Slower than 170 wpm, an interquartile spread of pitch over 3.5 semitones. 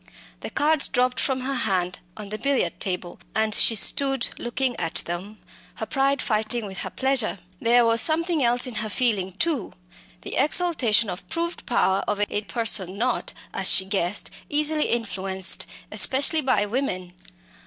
Yes: average, 160 wpm; average, 5.2 semitones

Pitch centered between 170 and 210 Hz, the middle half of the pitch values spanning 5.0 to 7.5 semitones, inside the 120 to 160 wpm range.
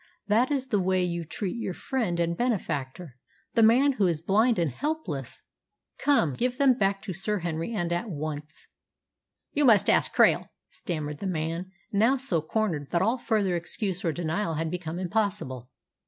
No: medium, 185 Hz; average, 5.3 semitones; average, 170 wpm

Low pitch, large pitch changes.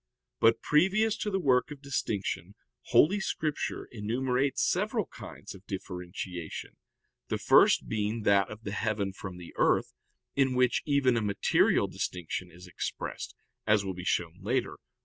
Yes: low, 110 Hz; wide, 6.0 semitones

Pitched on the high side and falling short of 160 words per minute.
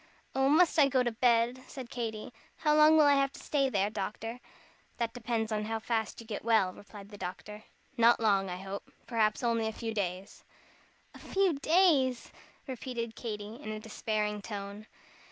No: high, 225 Hz; average, 180 wpm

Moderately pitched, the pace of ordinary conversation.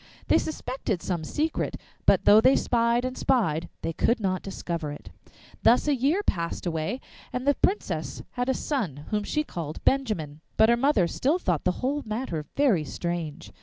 No: high, 220 Hz; average, 175 wpm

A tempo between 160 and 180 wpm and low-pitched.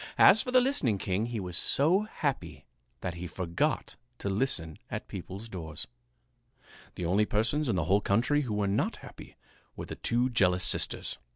Yes: average, 175 wpm; low, 105 Hz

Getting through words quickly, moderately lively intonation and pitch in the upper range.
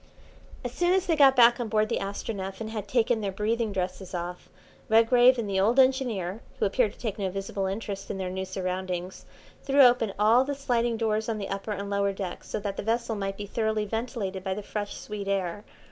Yes: fast, 220 wpm; average, 3.2 semitones; high, 210 Hz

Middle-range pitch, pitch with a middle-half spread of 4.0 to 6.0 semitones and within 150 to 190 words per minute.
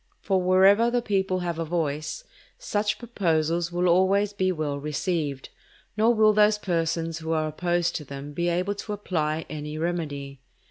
Yes: medium, 175 Hz; average, 4.3 semitones; average, 165 wpm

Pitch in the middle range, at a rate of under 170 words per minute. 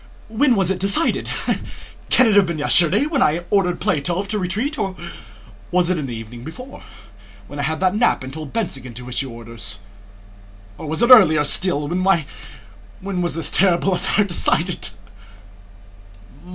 Yes: medium, 175 Hz; average, 160 wpm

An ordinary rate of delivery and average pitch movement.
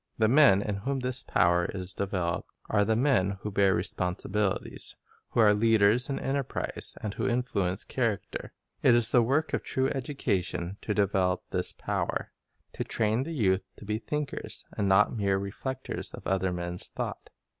Yes: average, 170 wpm; average, 4.5 semitones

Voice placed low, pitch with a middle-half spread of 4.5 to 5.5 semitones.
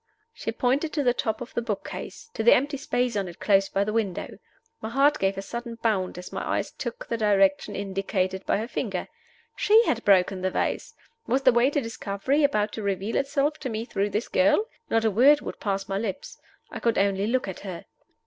No: high, 225 Hz; average, 4.9 semitones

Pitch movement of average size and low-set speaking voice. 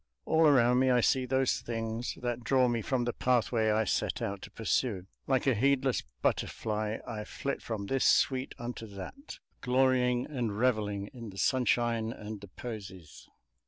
Yes: average, 3.0 semitones; low, 120 Hz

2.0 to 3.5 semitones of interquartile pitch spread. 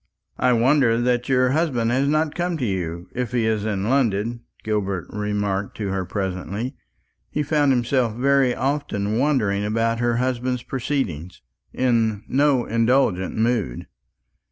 No: average, 4.2 semitones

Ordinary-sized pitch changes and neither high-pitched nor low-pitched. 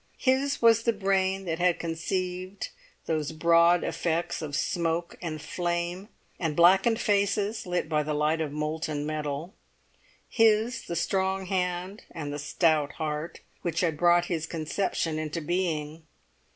Yes: average, 3.3 semitones; medium, 170 Hz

